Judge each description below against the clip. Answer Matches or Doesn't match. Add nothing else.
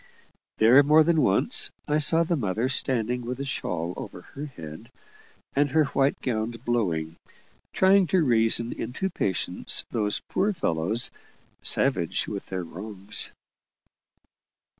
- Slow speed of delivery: Matches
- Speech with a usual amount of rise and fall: Doesn't match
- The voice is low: Matches